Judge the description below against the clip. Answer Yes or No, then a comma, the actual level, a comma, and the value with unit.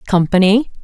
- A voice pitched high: Yes, high, 200 Hz